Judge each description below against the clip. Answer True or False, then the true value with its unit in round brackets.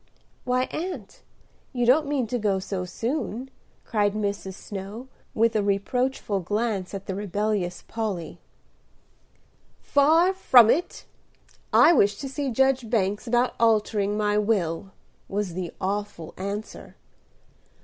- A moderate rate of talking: False (125 wpm)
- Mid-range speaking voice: False (210 Hz)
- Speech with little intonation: False (4.0 semitones)